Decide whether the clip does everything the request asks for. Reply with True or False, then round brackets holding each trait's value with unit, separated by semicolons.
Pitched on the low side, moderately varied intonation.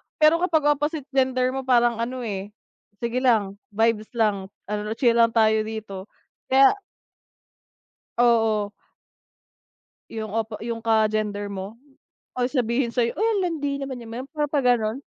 False (235 Hz; 3.4 semitones)